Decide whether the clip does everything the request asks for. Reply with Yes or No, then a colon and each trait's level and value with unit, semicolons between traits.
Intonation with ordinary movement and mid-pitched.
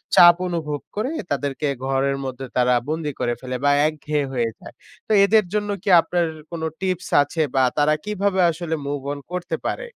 Yes: average, 4.7 semitones; medium, 155 Hz